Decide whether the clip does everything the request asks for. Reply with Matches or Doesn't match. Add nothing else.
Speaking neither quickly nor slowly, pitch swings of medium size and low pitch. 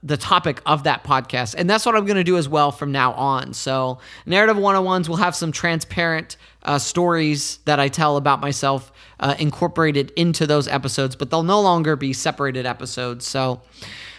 Doesn't match